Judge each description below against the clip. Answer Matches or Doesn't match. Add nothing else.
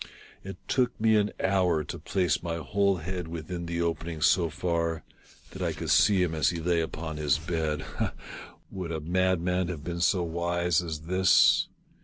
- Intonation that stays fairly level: Matches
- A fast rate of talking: Doesn't match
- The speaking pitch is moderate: Doesn't match